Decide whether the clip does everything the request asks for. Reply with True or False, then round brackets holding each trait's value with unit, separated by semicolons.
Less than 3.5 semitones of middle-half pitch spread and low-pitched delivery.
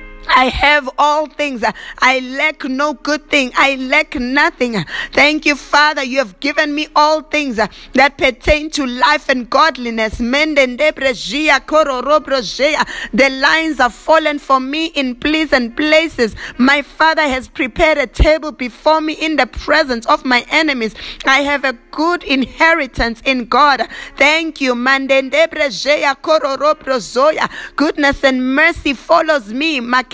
False (2.8 semitones; 285 Hz)